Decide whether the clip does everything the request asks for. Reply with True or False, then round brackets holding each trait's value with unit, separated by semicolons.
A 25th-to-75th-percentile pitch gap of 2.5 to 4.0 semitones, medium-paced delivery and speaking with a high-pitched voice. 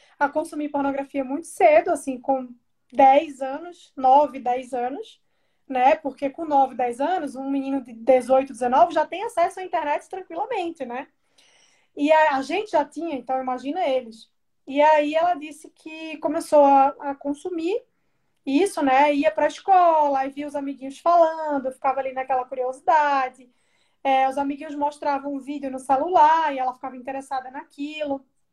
True (2.8 semitones; 155 wpm; 285 Hz)